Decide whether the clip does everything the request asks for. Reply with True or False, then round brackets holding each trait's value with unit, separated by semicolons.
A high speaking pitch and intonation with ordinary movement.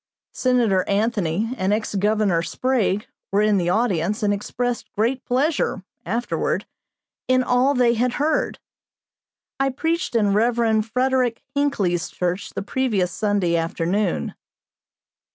True (220 Hz; 4.3 semitones)